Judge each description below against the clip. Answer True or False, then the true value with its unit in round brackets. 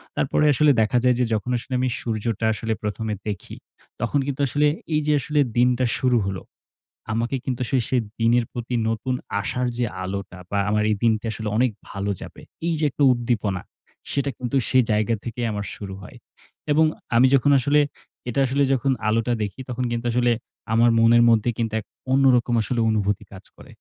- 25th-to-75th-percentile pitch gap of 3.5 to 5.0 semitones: False (2.8 semitones)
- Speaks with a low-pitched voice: True (120 Hz)